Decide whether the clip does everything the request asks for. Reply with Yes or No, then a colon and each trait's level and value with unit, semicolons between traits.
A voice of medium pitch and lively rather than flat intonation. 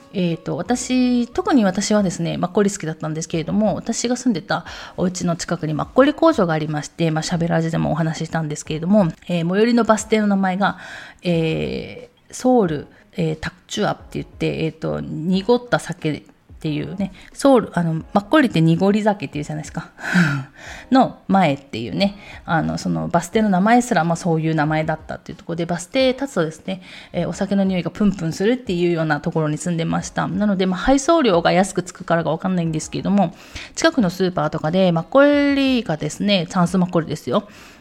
No: medium, 175 Hz; average, 4.8 semitones